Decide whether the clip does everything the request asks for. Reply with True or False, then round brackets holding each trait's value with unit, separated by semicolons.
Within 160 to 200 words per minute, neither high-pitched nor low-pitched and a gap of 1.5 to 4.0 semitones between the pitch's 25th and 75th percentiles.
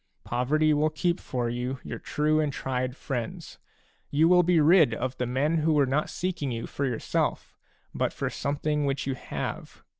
True (180 wpm; 145 Hz; 3.3 semitones)